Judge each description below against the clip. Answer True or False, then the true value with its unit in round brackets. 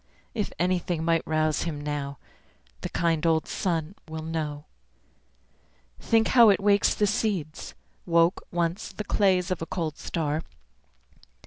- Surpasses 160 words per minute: False (135 wpm)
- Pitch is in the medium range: True (165 Hz)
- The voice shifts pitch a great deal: False (3.1 semitones)